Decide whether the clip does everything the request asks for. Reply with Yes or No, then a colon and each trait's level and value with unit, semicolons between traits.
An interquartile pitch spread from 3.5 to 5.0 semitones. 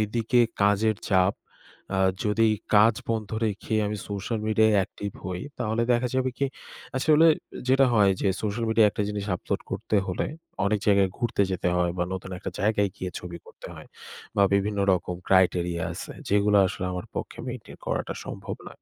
No: average, 3.0 semitones